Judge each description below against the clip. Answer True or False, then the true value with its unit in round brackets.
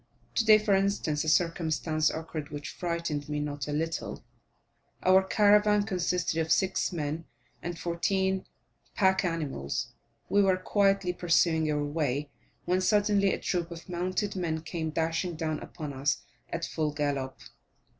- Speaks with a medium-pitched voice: True (170 Hz)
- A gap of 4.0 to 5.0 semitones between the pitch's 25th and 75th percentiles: False (3.6 semitones)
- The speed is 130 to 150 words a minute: True (145 wpm)